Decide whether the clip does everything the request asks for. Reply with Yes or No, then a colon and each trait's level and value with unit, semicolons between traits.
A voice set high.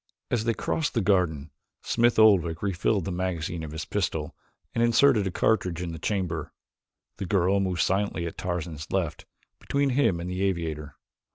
No: very low, 90 Hz